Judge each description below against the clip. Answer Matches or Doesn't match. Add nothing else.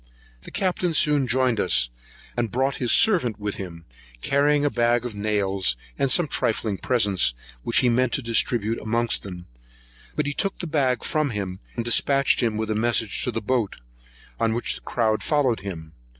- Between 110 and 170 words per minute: Doesn't match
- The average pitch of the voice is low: Matches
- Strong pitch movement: Doesn't match